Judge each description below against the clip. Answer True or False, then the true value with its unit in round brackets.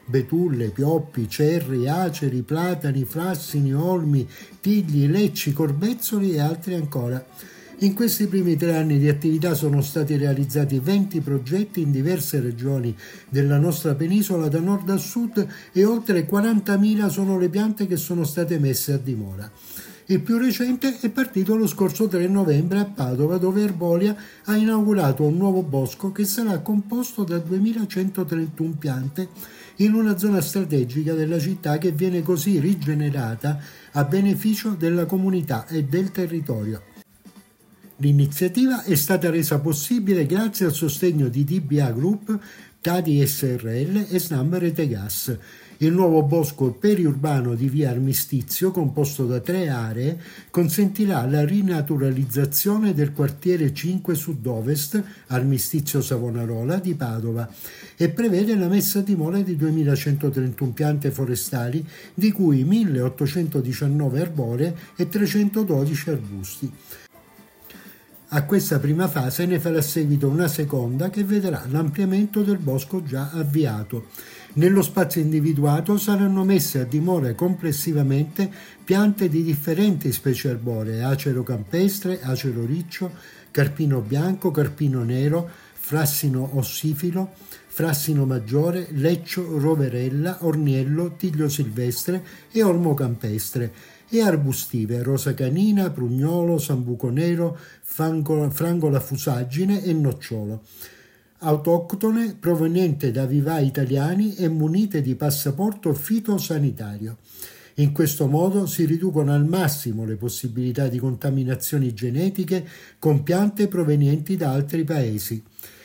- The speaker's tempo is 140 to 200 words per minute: False (120 wpm)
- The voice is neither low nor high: True (160 Hz)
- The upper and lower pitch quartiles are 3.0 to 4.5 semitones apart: False (5.2 semitones)